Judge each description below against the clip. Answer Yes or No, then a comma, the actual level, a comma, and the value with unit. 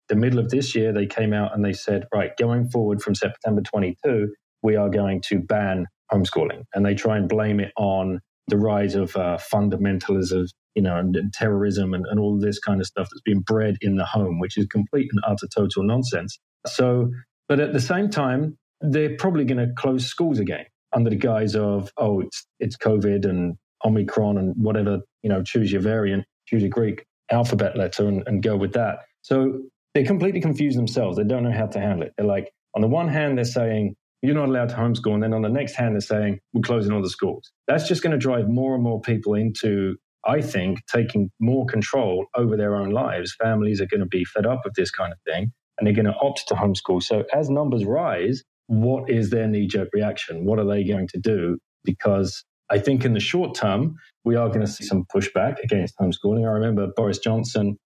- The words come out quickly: Yes, fast, 220 wpm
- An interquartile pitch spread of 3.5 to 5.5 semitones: No, average, 3.1 semitones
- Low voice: Yes, low, 105 Hz